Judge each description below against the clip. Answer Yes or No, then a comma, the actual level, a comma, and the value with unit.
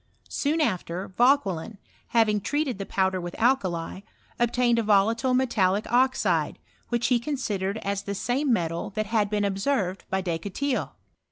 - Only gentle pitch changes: No, average, 4.4 semitones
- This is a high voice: Yes, high, 210 Hz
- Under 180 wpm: Yes, average, 150 wpm